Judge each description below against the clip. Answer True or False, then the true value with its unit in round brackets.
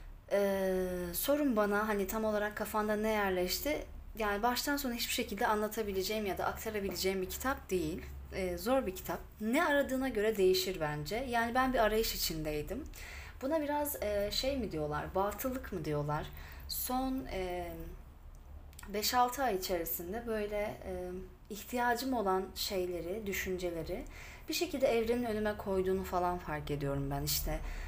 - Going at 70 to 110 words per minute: False (140 wpm)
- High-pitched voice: True (200 Hz)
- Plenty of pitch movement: False (4.7 semitones)